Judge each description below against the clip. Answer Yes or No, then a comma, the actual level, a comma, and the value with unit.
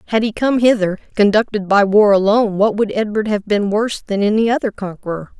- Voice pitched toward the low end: No, high, 210 Hz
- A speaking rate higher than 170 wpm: Yes, average, 200 wpm